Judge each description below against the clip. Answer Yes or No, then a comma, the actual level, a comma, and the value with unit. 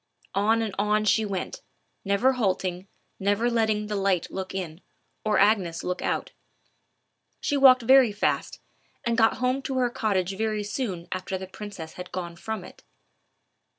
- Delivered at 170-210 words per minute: No, average, 155 wpm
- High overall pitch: Yes, high, 205 Hz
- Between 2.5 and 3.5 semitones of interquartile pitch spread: Yes, average, 3.2 semitones